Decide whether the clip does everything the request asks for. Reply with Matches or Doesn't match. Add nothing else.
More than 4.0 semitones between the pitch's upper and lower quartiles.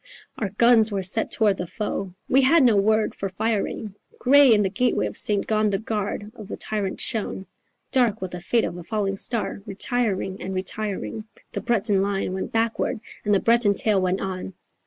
Doesn't match